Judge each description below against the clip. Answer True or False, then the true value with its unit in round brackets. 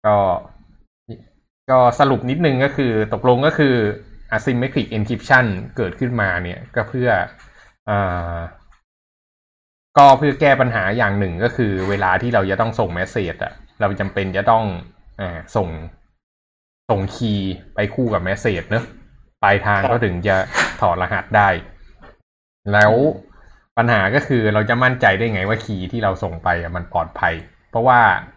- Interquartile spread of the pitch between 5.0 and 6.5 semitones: False (4.3 semitones)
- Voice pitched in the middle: False (105 Hz)